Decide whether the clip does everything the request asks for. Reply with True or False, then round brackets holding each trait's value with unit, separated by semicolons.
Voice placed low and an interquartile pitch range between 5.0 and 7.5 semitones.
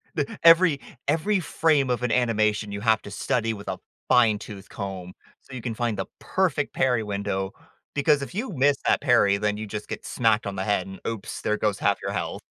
True (110 Hz; 5.4 semitones)